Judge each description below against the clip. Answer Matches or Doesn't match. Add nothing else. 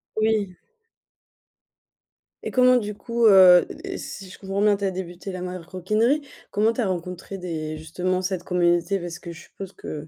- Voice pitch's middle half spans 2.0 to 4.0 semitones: Matches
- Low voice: Doesn't match